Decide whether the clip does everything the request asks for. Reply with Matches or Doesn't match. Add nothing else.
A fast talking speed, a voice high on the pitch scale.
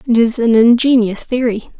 Doesn't match